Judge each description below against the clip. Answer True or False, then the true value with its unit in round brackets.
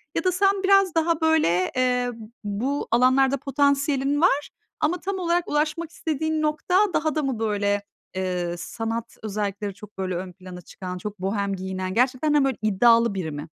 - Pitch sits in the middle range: False (250 Hz)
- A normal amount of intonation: False (7.6 semitones)